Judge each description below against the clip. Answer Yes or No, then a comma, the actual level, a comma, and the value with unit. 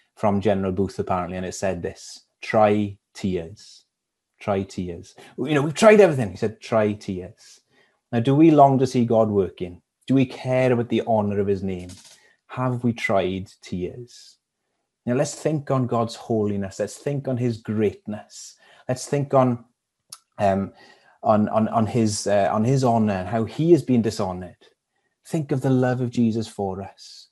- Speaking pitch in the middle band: No, low, 110 Hz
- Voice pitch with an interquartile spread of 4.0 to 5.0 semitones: Yes, average, 4.5 semitones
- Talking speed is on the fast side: No, average, 175 wpm